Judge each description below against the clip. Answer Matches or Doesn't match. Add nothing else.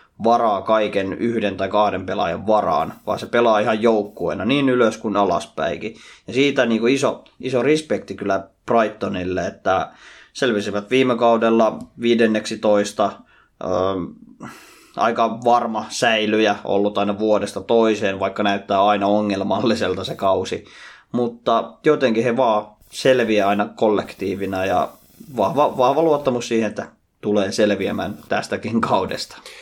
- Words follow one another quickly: Doesn't match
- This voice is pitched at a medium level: Doesn't match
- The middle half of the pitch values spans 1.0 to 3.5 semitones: Matches